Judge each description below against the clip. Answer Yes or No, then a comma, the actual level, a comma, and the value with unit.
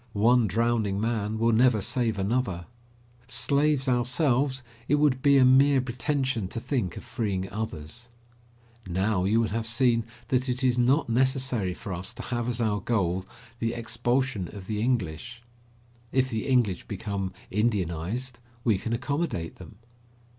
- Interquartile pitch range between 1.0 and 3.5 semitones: No, average, 4.1 semitones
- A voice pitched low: Yes, low, 115 Hz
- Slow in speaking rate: No, average, 150 wpm